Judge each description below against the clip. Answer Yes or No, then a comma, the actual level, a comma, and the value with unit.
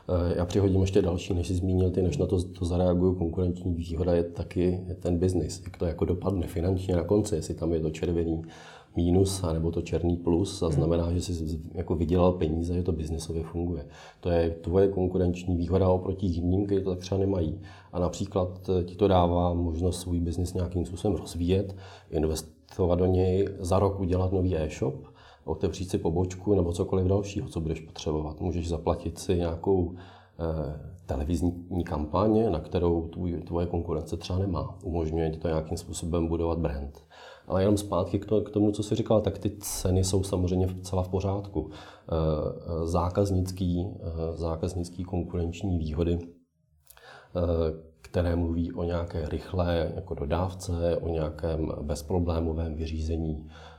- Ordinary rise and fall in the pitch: No, narrow, 2.0 semitones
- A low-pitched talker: Yes, very low, 90 Hz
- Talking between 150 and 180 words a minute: Yes, average, 160 wpm